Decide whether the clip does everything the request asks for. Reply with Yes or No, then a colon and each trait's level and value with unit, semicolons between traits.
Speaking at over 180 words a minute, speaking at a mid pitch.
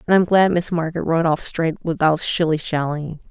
Yes: average, 200 wpm; medium, 165 Hz